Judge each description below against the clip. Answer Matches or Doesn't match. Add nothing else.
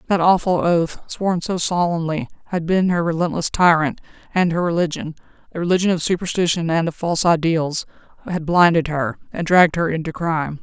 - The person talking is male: Doesn't match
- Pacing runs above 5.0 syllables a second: Matches